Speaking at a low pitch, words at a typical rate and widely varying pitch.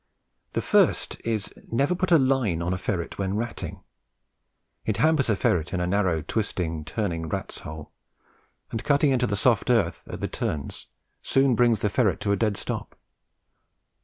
Yes: low, 105 Hz; average, 170 wpm; wide, 5.9 semitones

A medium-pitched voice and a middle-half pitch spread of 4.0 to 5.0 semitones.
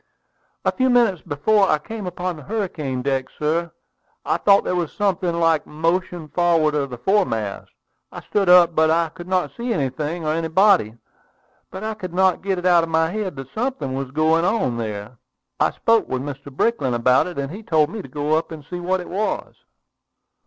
Yes: medium, 165 Hz; average, 4.6 semitones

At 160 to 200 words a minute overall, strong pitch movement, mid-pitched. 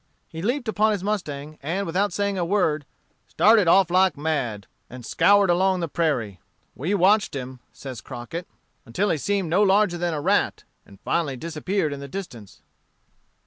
Yes: average, 170 wpm; wide, 5.7 semitones; medium, 170 Hz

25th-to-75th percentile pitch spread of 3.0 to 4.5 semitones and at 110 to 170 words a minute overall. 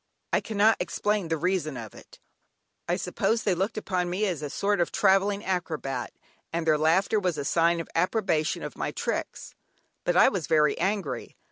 No: average, 4.0 semitones; average, 180 wpm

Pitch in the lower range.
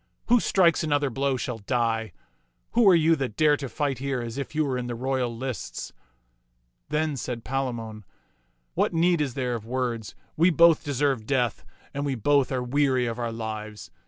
Yes: low, 130 Hz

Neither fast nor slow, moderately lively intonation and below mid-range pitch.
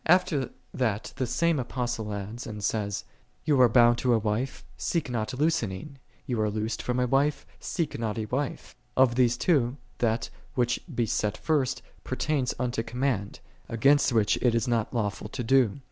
Yes: average, 175 wpm; average, 3.5 semitones; low, 120 Hz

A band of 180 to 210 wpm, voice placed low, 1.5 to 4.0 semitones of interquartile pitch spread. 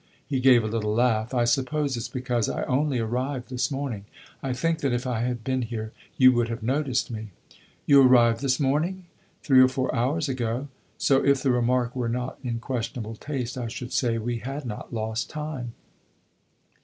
Yes: average, 190 wpm; low, 125 Hz; narrow, 2.5 semitones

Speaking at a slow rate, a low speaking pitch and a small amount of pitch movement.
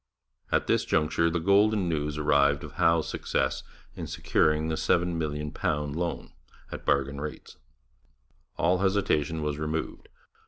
Yes: slow, 125 wpm; very low, 80 Hz; narrow, 2.3 semitones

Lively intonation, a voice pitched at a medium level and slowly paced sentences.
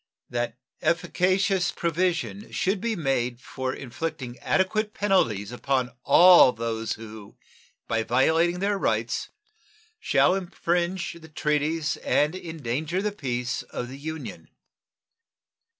Yes: wide, 6.8 semitones; medium, 160 Hz; slow, 115 wpm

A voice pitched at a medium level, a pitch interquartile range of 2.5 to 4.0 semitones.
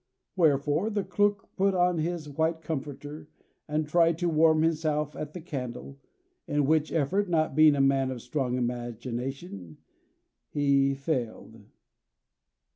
Yes: medium, 150 Hz; average, 3.4 semitones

